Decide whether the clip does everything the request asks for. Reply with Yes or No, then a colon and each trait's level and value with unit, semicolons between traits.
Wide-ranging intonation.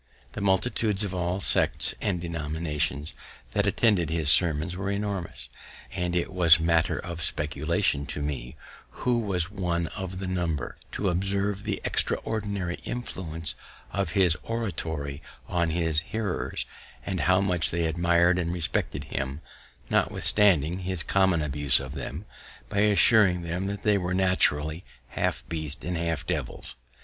No: average, 3.2 semitones